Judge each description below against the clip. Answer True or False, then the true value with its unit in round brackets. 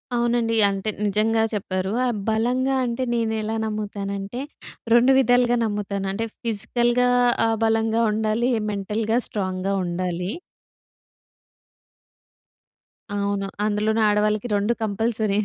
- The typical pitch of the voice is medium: False (215 Hz)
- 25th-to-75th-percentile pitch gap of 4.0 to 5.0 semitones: False (2.6 semitones)